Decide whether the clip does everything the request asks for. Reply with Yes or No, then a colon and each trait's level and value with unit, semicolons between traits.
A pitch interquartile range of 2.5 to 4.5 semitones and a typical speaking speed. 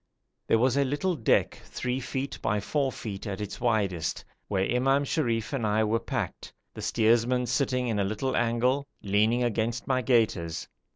Yes: average, 3.3 semitones; average, 170 wpm